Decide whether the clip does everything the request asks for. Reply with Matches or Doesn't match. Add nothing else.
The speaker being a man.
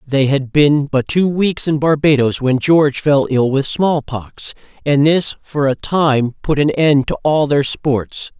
Matches